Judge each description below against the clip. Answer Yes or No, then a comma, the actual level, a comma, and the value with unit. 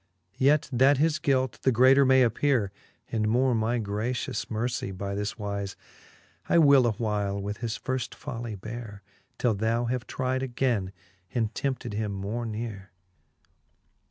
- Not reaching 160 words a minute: Yes, average, 150 wpm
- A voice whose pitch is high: No, low, 115 Hz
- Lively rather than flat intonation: No, average, 3.9 semitones